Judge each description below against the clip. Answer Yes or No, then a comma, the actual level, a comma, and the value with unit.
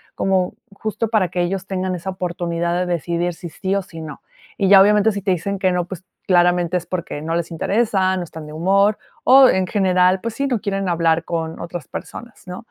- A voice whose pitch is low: No, medium, 185 Hz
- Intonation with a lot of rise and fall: No, narrow, 2.4 semitones